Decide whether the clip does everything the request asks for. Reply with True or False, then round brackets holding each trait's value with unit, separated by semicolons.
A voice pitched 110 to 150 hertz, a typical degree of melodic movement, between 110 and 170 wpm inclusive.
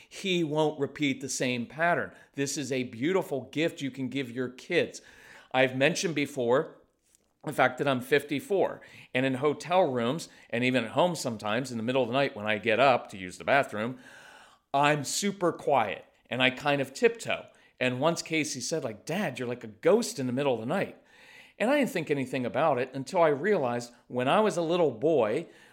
False (140 Hz; 4.6 semitones; 205 wpm)